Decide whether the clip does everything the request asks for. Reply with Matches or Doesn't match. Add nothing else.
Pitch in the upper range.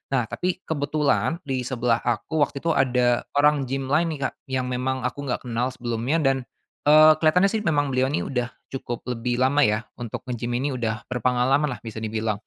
Doesn't match